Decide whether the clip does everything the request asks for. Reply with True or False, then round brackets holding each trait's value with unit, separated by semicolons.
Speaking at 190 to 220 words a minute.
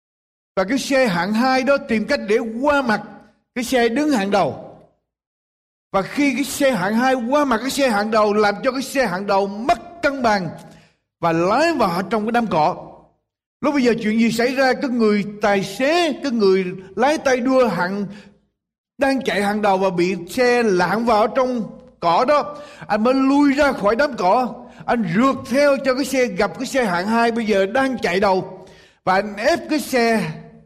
True (200 wpm)